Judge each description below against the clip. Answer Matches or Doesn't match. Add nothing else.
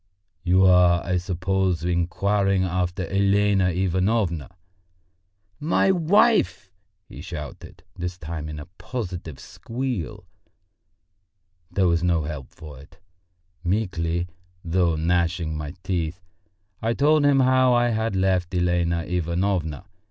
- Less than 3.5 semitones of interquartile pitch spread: Matches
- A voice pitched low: Matches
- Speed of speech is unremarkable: Doesn't match